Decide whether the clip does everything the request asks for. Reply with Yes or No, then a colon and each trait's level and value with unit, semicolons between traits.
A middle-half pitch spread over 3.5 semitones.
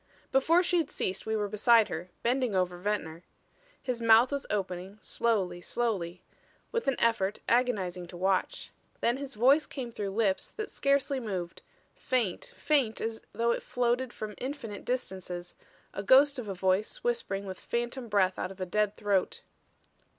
Yes: average, 5.0 semitones